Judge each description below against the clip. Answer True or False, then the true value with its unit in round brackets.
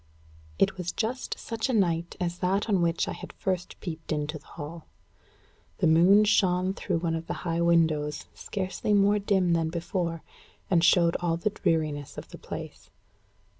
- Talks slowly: False (170 wpm)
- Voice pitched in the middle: True (170 Hz)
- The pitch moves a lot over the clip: False (2.6 semitones)